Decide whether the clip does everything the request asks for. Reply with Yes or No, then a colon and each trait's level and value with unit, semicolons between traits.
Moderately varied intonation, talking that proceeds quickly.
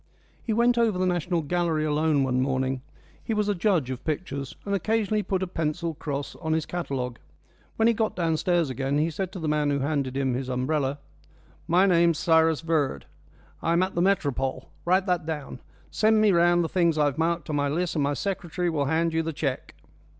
Yes: average, 4.0 semitones; fast, 210 wpm